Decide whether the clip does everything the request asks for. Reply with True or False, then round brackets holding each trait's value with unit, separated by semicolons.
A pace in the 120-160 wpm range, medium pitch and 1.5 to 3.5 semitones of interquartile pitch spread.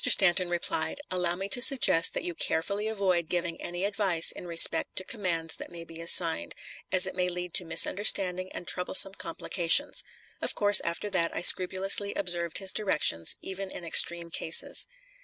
False (170 wpm; 180 Hz; 2.4 semitones)